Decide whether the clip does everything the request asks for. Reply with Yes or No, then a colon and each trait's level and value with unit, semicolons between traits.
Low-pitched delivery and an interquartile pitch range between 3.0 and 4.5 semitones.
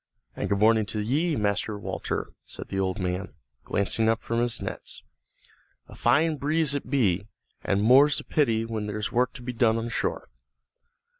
Yes: low, 115 Hz; average, 4.0 semitones